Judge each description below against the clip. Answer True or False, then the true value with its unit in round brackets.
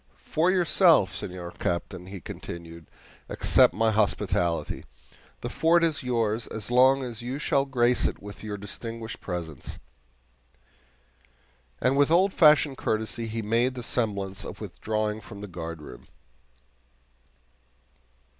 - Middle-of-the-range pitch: False (110 Hz)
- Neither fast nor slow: False (125 wpm)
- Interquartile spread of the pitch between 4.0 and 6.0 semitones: True (5.2 semitones)